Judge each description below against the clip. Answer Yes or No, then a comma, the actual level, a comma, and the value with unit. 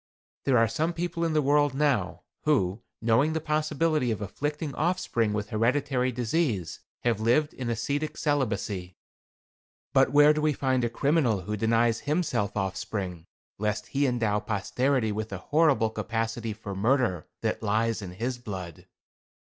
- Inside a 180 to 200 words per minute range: No, average, 150 wpm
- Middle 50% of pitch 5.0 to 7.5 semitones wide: Yes, wide, 5.5 semitones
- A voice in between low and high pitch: No, low, 120 Hz